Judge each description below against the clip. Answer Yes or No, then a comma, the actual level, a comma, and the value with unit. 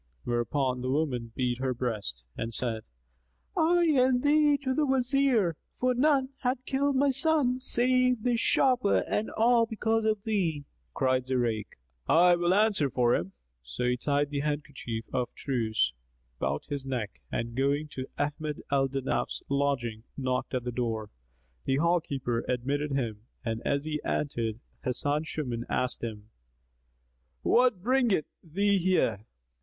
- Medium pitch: Yes, medium, 145 Hz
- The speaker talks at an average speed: Yes, average, 150 wpm